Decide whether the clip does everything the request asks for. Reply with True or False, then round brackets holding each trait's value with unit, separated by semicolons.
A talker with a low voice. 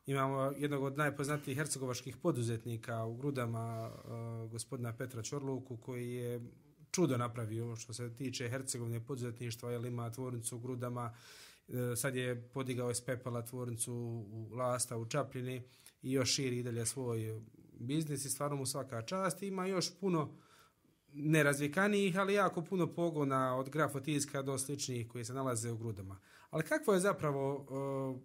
True (130 Hz)